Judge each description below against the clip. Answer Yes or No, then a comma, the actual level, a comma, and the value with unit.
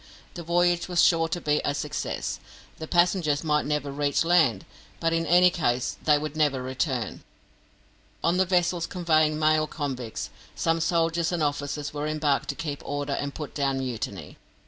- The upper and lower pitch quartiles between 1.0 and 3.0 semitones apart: Yes, average, 2.7 semitones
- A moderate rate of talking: Yes, average, 170 wpm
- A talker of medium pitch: Yes, medium, 155 Hz